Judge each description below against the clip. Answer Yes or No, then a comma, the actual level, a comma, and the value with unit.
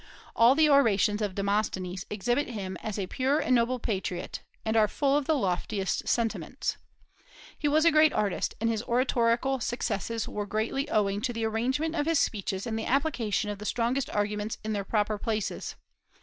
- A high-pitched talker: Yes, high, 225 Hz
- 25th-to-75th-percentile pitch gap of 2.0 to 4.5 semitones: Yes, average, 4.0 semitones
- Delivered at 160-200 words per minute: Yes, average, 180 wpm